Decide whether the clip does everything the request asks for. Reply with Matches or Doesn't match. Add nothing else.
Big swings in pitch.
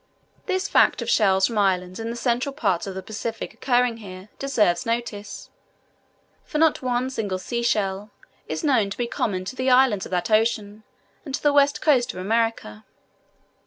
Doesn't match